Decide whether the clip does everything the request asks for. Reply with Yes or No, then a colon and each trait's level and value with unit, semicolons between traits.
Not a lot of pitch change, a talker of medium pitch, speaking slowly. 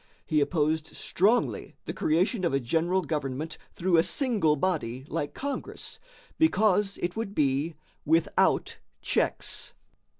No: average, 4.4 semitones; medium, 165 Hz; slow, 125 wpm